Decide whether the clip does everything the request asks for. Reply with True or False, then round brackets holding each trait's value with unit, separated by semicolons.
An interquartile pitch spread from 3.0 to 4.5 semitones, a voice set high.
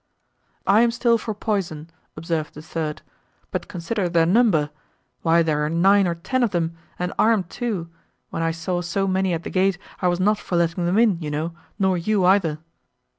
False (3.4 semitones; 175 Hz)